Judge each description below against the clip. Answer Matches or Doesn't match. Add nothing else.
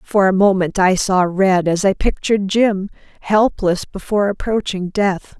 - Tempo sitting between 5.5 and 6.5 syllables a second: Doesn't match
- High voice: Matches